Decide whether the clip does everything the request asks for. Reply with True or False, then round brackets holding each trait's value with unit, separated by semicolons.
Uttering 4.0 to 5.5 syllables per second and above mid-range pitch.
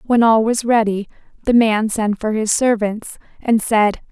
True (4.2 syllables/s; 220 Hz)